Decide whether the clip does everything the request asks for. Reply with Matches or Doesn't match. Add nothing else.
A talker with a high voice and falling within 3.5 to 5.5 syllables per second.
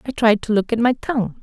Doesn't match